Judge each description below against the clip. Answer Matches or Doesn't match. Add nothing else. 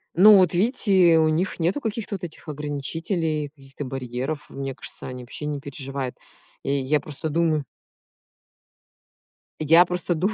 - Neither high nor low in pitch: Matches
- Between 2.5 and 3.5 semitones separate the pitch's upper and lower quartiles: Doesn't match